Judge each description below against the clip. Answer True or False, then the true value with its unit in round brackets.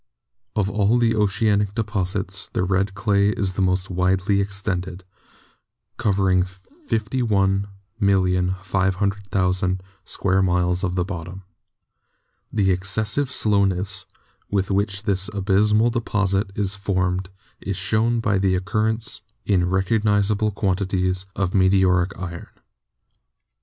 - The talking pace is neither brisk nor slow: False (110 wpm)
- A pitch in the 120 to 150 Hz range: False (95 Hz)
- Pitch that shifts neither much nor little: False (1.8 semitones)